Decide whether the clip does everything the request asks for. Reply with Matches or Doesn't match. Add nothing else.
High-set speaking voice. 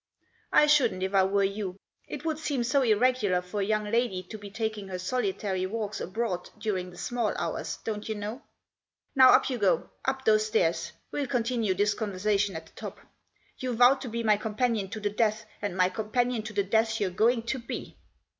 Matches